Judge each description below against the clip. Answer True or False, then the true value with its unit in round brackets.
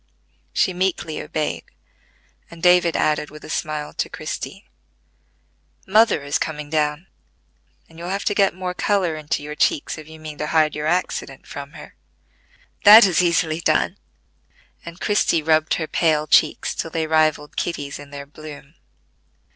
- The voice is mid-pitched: True (155 Hz)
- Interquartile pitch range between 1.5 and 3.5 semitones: True (2.5 semitones)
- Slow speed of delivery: False (155 wpm)